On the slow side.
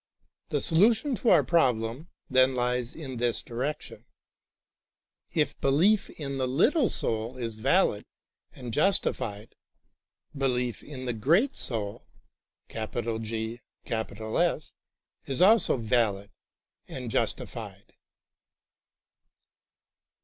Yes: slow, 90 wpm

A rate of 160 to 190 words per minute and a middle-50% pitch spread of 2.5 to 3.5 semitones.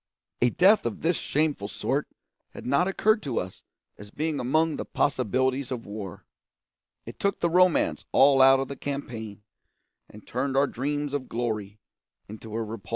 No: average, 170 wpm; average, 4.9 semitones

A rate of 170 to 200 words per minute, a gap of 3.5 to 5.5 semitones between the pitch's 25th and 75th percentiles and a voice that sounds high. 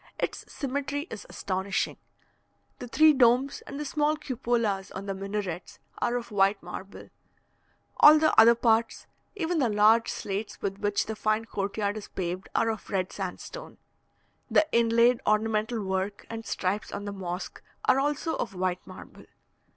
No: average, 160 wpm; average, 4.0 semitones; high, 220 Hz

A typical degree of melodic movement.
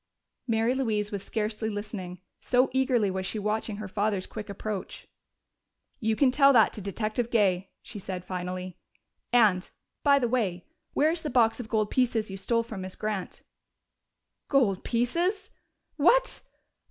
Yes: average, 4.0 semitones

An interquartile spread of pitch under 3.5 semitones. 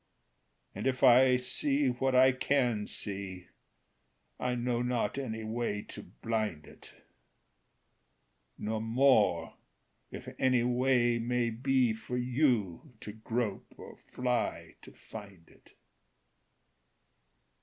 Yes: average, 2.7 semitones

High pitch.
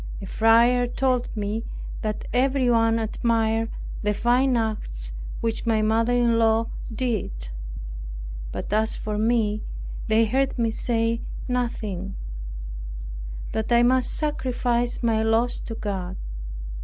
Yes: high, 225 Hz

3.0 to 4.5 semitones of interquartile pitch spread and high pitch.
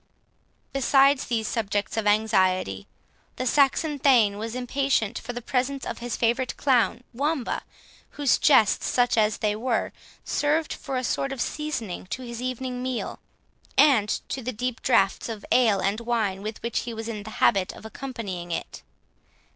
Yes: average, 3.5 semitones; high, 235 Hz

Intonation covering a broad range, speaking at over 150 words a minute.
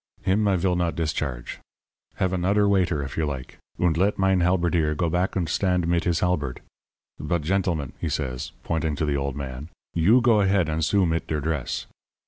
No: average, 3.6 semitones; average, 190 wpm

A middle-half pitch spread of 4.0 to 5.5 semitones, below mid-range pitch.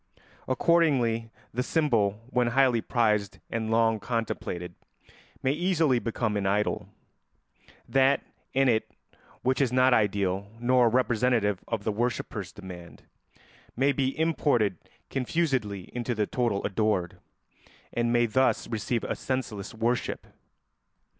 No: average, 3.6 semitones; low, 120 Hz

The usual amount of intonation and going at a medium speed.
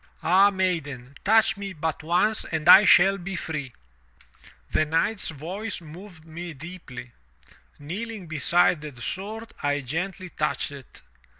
No: average, 4.4 semitones; slow, 130 wpm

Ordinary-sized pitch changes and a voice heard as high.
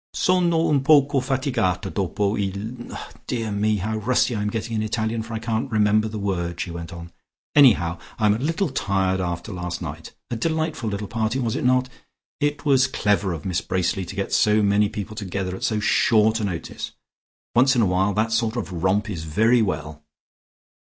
No: average, 3.9 semitones; low, 105 Hz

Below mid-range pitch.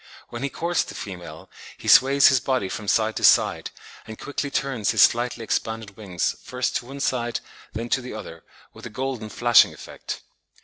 Yes: low, 120 Hz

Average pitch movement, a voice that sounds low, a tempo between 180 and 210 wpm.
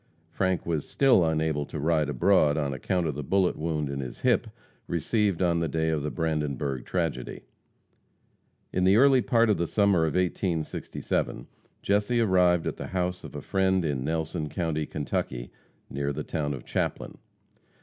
No: average, 4.0 semitones; very low, 80 Hz; average, 170 wpm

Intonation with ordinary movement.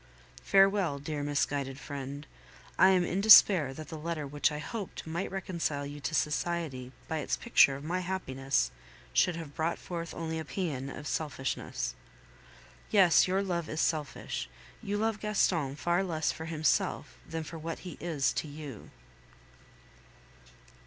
Yes: average, 3.9 semitones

